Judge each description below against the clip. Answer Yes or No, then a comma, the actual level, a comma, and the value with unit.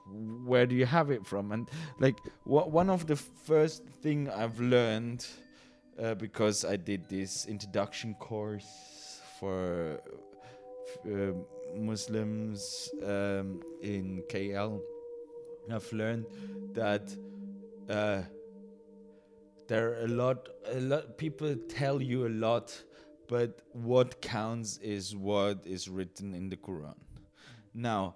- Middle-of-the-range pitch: No, low, 115 Hz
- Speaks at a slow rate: Yes, slow, 115 wpm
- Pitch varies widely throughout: Yes, wide, 7.0 semitones